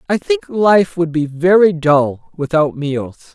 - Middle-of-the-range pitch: Yes, medium, 165 Hz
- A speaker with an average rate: Yes, average, 160 wpm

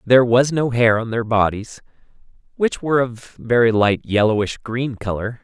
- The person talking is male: Yes, male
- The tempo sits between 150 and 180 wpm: Yes, average, 175 wpm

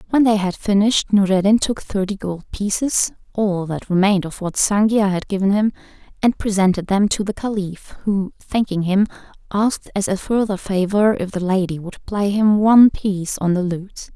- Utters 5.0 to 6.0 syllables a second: No, 4.4 syllables/s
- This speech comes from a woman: Yes, female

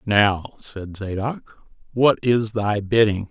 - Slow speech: Yes, slow, 125 wpm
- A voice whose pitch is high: No, low, 105 Hz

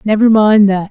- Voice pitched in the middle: No, high, 210 Hz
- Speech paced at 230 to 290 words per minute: No, average, 200 wpm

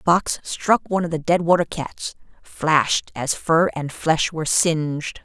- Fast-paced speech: No, average, 185 wpm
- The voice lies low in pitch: No, medium, 160 Hz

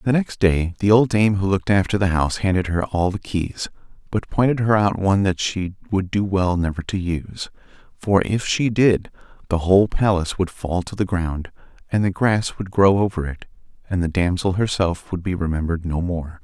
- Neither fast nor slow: No, fast, 210 wpm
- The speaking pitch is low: Yes, very low, 95 Hz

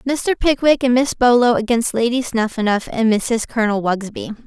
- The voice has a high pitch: Yes, high, 235 Hz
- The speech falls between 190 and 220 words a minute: No, average, 160 wpm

